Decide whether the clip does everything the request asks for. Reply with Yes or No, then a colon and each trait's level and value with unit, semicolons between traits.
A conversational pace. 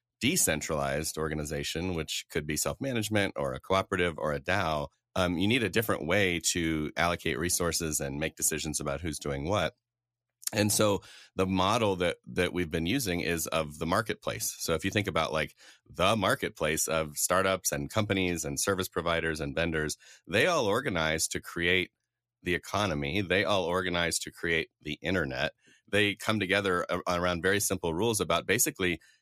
Yes: average, 170 wpm